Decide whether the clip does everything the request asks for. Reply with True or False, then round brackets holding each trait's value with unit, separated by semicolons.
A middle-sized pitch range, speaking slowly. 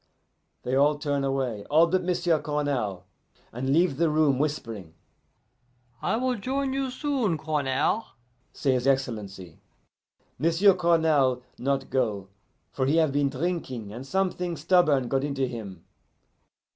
True (4.8 semitones; 130 wpm)